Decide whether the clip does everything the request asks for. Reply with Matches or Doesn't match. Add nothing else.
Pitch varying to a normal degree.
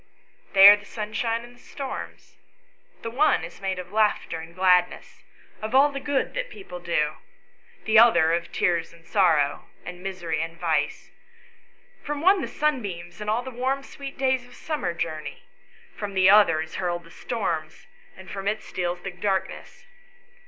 Doesn't match